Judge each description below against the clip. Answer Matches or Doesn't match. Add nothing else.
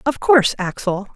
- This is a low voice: Doesn't match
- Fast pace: Doesn't match